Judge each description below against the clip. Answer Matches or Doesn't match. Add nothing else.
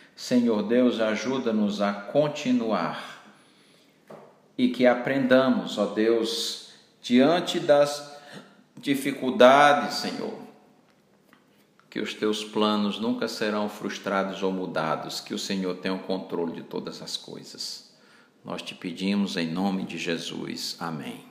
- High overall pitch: Doesn't match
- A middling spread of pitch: Doesn't match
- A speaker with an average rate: Doesn't match